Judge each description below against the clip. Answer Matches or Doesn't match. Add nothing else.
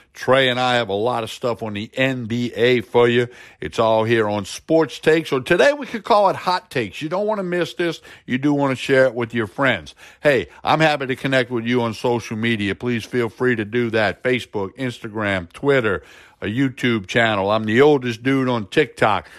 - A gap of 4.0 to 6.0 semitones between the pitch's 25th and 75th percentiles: Doesn't match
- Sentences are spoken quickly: Matches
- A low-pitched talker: Matches